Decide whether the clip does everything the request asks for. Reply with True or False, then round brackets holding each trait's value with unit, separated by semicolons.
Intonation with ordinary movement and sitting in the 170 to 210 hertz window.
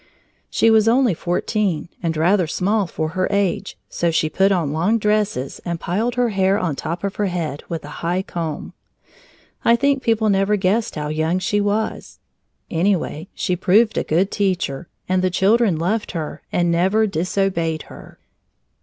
True (3.9 semitones; 185 Hz)